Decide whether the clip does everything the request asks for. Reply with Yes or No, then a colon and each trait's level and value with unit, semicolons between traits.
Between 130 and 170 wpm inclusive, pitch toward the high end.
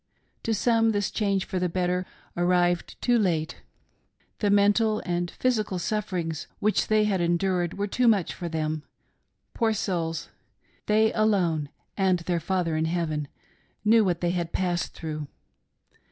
No: average, 150 wpm; medium, 180 Hz